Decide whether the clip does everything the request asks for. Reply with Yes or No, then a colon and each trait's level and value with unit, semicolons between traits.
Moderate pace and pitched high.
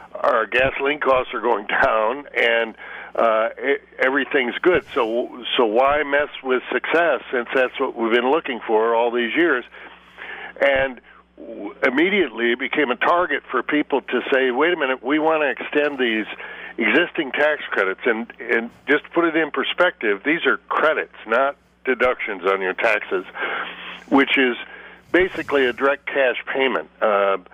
No: average, 160 wpm; low, 135 Hz